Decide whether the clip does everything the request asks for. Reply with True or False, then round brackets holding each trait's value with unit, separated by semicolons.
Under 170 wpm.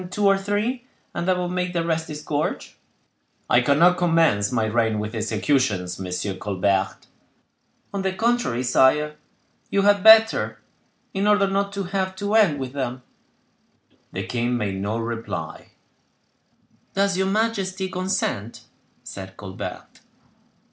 True (135 wpm)